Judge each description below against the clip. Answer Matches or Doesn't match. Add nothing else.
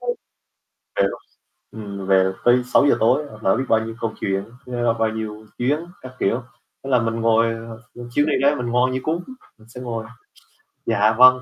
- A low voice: Matches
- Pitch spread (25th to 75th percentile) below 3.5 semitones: Matches